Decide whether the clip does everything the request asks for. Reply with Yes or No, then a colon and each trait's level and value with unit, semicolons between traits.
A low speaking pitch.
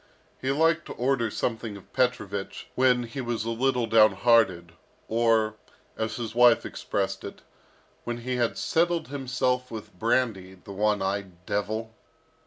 Yes: low, 115 Hz